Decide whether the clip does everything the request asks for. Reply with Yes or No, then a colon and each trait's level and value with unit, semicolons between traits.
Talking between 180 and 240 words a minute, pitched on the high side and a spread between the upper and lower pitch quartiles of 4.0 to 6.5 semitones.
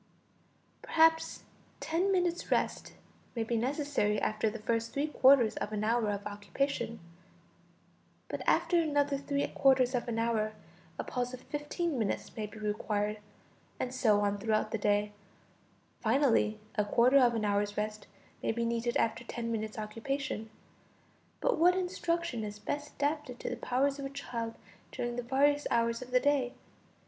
No: average, 160 wpm; high, 240 Hz; average, 4.7 semitones